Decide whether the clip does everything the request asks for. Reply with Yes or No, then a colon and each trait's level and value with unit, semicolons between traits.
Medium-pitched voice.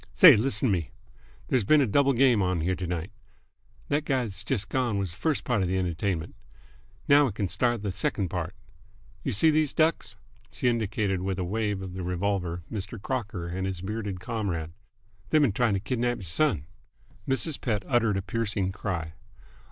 No: low, 100 Hz